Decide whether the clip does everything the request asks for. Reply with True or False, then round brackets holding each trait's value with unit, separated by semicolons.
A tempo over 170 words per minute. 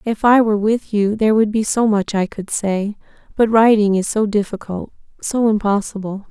True (190 wpm)